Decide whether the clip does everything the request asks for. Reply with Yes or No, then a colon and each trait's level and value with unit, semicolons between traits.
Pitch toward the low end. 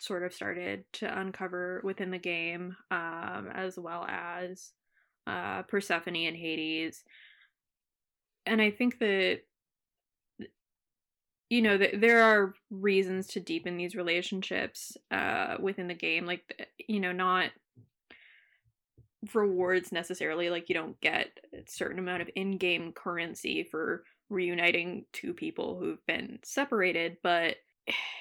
No: medium, 180 Hz